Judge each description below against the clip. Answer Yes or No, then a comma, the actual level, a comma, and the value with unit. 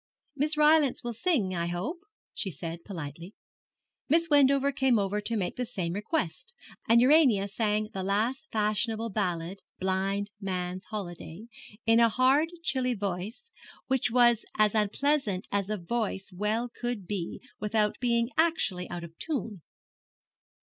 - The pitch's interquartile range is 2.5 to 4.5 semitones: No, average, 5.0 semitones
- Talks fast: No, average, 145 wpm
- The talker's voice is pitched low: No, high, 215 Hz